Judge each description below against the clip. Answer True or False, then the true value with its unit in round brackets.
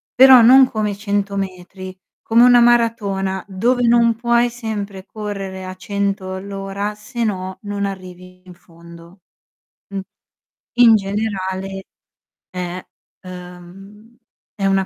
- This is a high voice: True (200 Hz)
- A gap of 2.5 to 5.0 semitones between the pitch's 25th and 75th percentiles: True (2.9 semitones)